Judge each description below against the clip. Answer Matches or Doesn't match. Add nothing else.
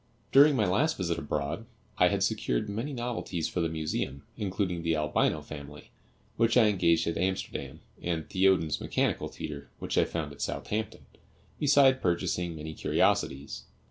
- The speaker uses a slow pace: Doesn't match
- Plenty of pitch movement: Matches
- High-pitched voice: Doesn't match